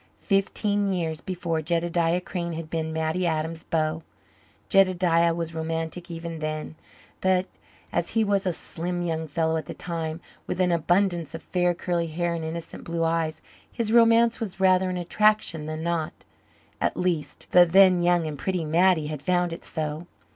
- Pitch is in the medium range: Yes, medium, 170 Hz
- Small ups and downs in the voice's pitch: Yes, narrow, 2.1 semitones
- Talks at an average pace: Yes, average, 170 wpm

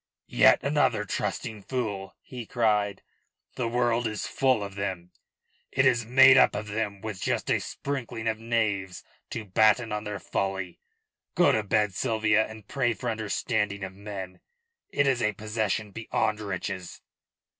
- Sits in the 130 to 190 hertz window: No, low, 110 Hz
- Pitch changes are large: No, narrow, 2.6 semitones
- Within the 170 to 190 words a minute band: No, average, 155 wpm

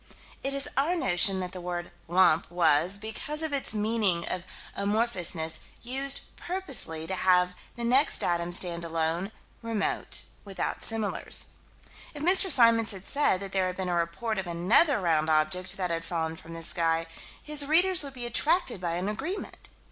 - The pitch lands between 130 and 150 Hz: No, high, 190 Hz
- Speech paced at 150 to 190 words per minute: Yes, average, 170 wpm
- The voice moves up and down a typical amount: No, wide, 6.4 semitones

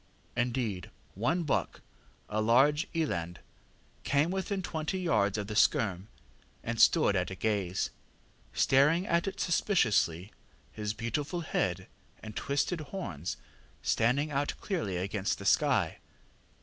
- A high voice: No, low, 120 Hz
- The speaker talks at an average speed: No, slow, 120 wpm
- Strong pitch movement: Yes, wide, 7.9 semitones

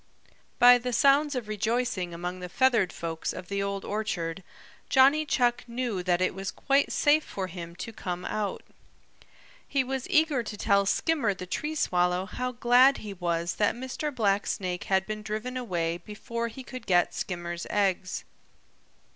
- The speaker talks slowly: No, average, 165 wpm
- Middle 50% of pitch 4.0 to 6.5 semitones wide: Yes, wide, 5.6 semitones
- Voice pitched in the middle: No, high, 210 Hz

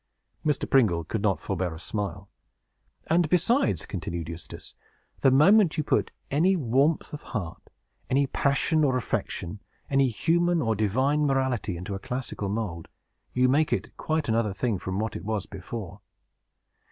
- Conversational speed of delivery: Yes, average, 155 wpm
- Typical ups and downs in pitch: No, wide, 6.8 semitones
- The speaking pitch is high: No, low, 120 Hz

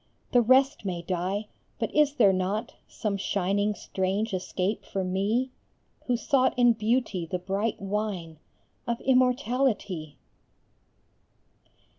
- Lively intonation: No, average, 4.5 semitones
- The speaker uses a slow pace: Yes, slow, 115 wpm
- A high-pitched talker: Yes, high, 205 Hz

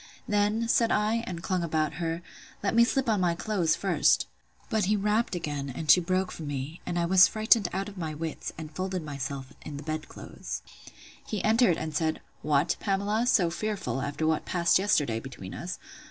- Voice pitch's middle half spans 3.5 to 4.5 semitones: No, average, 5.0 semitones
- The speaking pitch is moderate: Yes, medium, 175 Hz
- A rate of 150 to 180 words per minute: No, average, 195 wpm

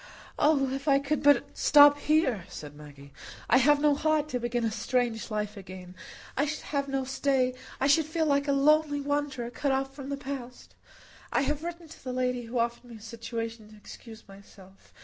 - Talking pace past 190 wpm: Yes, average, 200 wpm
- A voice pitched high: Yes, very high, 265 Hz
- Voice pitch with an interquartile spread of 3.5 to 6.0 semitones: Yes, average, 4.0 semitones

